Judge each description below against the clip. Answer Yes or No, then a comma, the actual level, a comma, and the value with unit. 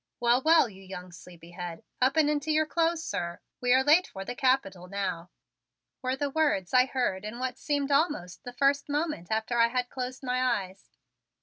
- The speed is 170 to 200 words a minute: Yes, average, 190 wpm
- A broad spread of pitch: Yes, wide, 6.8 semitones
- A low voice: No, very high, 250 Hz